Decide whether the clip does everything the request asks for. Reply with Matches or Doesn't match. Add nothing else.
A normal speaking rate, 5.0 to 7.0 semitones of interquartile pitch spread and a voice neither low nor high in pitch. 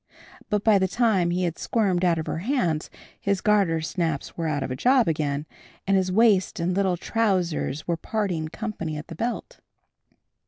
Doesn't match